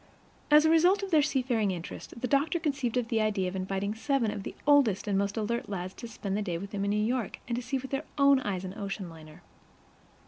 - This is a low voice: No, high, 220 Hz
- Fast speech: Yes, fast, 230 wpm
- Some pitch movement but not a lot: No, wide, 5.7 semitones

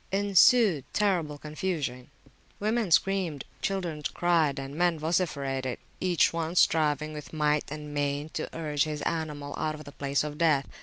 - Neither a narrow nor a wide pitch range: Yes, average, 3.1 semitones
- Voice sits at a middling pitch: Yes, medium, 155 Hz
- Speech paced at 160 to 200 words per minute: No, average, 150 wpm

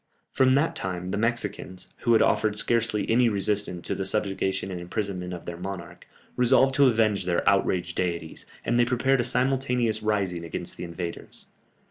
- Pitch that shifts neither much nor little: Yes, average, 4.8 semitones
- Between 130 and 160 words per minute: No, average, 170 wpm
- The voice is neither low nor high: No, low, 105 Hz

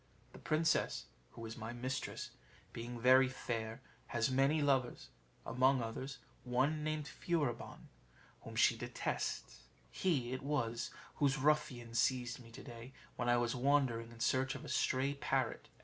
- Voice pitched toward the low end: Yes, low, 130 Hz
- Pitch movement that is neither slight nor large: Yes, average, 3.0 semitones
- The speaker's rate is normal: Yes, average, 150 wpm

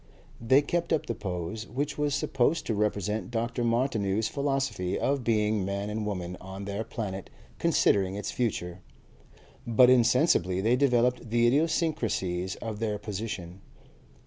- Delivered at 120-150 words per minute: Yes, average, 140 wpm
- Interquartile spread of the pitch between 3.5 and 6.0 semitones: Yes, average, 4.2 semitones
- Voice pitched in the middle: No, low, 110 Hz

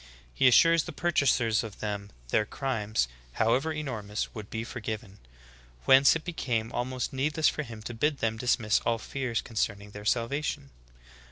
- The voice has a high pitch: No, low, 120 Hz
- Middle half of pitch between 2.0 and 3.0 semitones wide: No, average, 4.2 semitones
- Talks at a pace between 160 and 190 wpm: Yes, average, 170 wpm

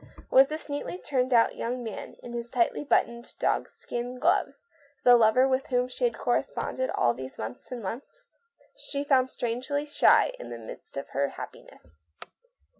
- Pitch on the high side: Yes, very high, 250 Hz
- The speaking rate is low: No, average, 170 wpm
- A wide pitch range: No, average, 3.3 semitones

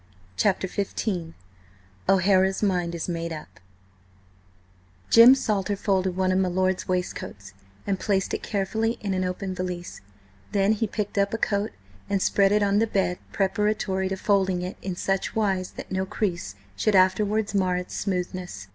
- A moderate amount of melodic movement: No, narrow, 1.8 semitones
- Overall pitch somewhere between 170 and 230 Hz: Yes, high, 190 Hz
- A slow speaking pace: No, average, 160 wpm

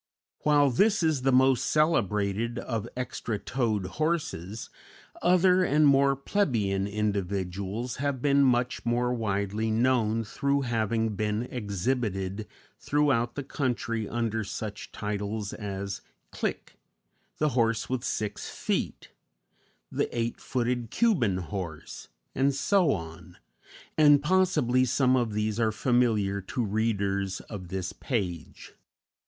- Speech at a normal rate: No, slow, 120 wpm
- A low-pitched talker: Yes, low, 115 Hz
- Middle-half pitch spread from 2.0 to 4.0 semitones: No, average, 4.6 semitones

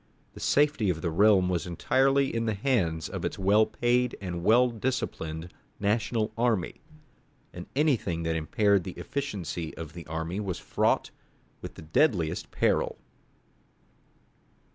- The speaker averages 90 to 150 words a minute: Yes, average, 140 wpm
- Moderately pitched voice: No, low, 100 Hz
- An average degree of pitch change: No, wide, 6.0 semitones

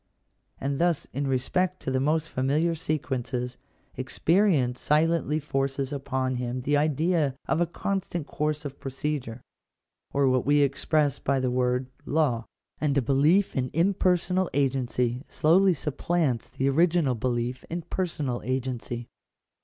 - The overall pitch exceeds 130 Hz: Yes, medium, 140 Hz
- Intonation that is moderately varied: Yes, average, 3.9 semitones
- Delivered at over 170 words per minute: No, average, 140 wpm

